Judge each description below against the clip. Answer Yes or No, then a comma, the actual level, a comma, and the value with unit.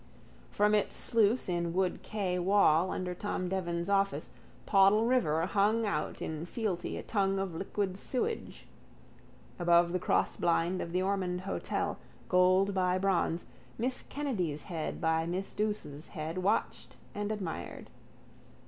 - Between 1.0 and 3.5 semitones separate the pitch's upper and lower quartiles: Yes, average, 3.0 semitones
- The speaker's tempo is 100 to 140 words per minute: Yes, slow, 135 wpm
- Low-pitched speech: No, medium, 185 Hz